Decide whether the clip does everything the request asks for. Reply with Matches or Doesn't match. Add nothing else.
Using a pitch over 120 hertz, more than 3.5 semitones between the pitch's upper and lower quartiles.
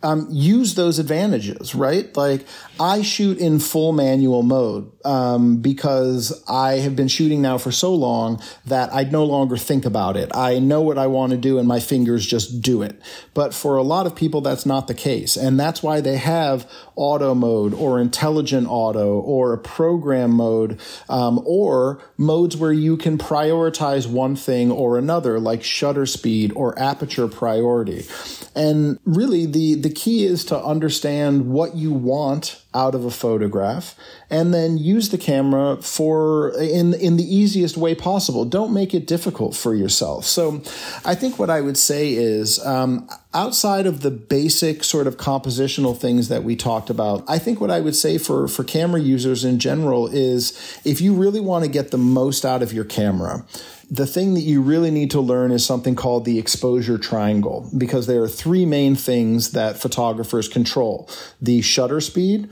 Matches